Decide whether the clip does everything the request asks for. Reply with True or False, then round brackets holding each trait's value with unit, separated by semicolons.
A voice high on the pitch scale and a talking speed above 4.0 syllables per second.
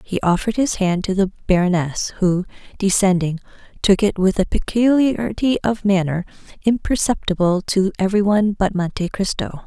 True (195 Hz; 5.2 syllables/s)